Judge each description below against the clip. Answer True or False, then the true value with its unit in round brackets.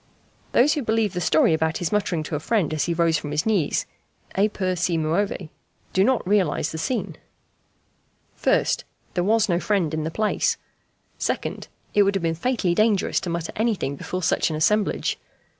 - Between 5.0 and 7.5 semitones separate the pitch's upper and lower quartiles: False (4.6 semitones)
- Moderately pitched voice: True (180 Hz)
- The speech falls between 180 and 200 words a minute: True (185 wpm)